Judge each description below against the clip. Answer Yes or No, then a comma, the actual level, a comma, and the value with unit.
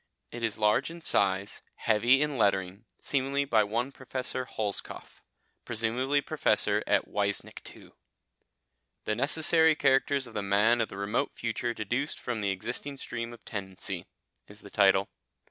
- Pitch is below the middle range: Yes, low, 115 Hz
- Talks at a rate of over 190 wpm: No, average, 145 wpm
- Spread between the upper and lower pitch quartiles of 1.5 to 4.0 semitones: No, average, 4.6 semitones